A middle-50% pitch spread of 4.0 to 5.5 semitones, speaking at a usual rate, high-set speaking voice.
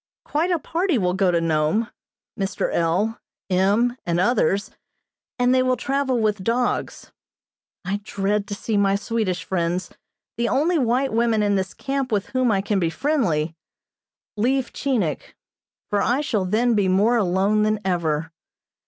Yes: average, 4.7 semitones; average, 155 wpm; high, 210 Hz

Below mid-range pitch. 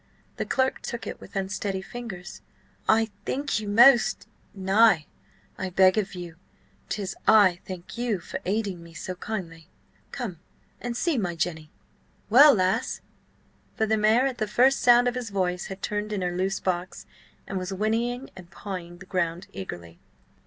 No: high, 195 Hz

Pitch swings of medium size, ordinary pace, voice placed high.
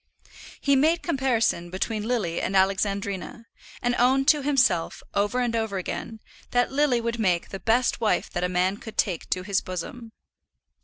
Yes: average, 4.6 semitones; average, 165 wpm; high, 220 Hz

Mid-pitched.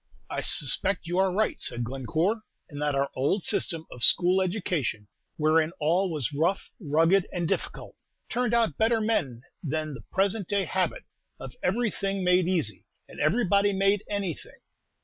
Yes: medium, 175 Hz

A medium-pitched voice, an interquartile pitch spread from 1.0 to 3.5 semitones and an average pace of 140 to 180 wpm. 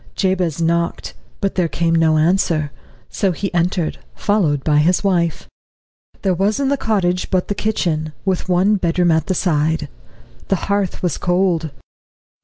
Yes: medium, 175 Hz; average, 2.9 semitones; average, 155 wpm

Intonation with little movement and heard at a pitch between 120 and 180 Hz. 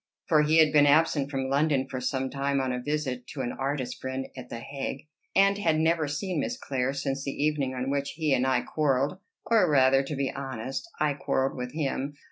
Yes: narrow, 2.3 semitones; medium, 140 Hz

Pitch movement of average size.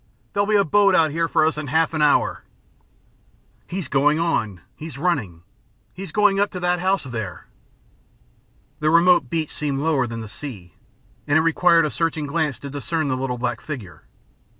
Yes: average, 4.5 semitones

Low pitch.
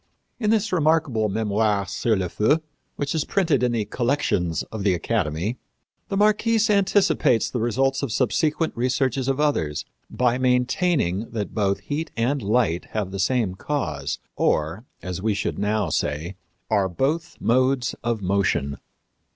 Yes: low, 115 Hz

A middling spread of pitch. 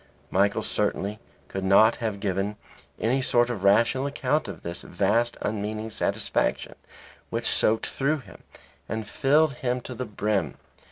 Yes: average, 4.0 semitones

